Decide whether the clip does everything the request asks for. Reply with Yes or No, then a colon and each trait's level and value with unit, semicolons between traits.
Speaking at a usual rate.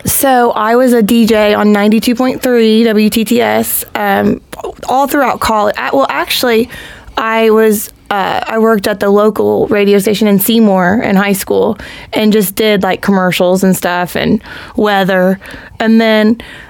Yes: average, 155 wpm